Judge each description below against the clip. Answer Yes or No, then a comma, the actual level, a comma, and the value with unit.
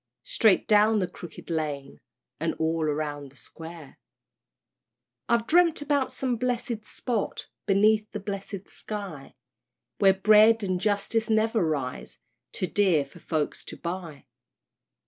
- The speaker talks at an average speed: No, slow, 125 wpm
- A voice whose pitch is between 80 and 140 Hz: No, high, 195 Hz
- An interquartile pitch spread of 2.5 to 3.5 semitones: No, wide, 5.4 semitones